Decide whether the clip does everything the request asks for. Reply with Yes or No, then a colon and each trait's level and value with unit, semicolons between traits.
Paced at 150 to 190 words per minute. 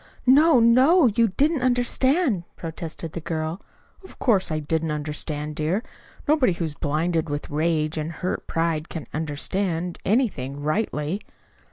No: average, 140 wpm